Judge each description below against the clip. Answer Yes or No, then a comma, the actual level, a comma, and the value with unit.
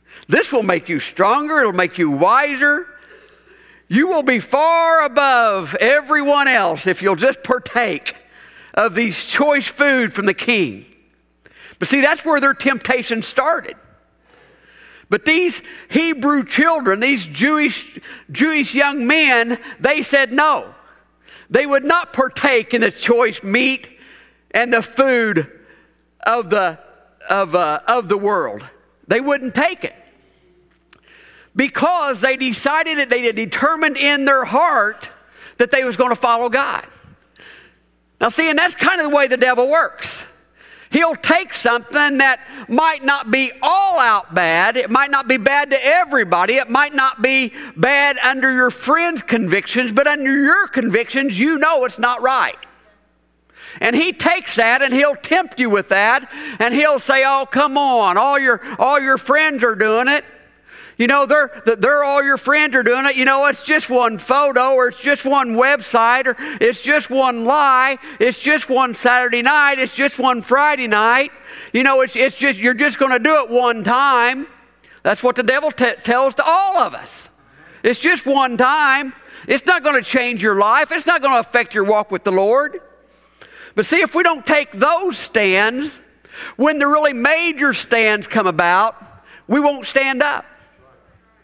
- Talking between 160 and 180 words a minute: Yes, average, 165 wpm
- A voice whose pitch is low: No, very high, 270 Hz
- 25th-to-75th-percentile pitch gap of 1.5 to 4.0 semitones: Yes, average, 3.4 semitones